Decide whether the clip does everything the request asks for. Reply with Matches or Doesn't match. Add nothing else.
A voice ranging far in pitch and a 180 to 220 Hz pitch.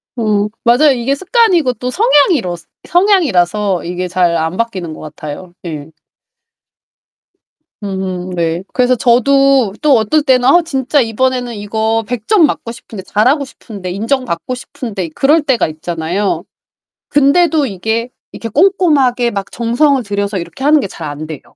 Doesn't match